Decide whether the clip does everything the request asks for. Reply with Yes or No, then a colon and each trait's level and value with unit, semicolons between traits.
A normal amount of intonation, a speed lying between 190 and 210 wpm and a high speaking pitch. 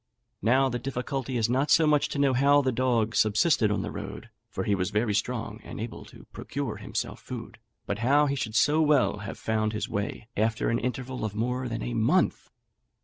No: average, 3.8 semitones; fast, 205 wpm; low, 120 Hz